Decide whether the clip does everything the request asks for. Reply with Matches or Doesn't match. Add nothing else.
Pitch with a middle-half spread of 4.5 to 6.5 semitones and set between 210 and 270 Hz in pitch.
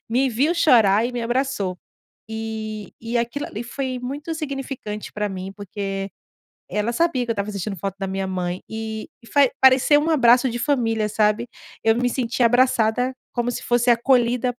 Doesn't match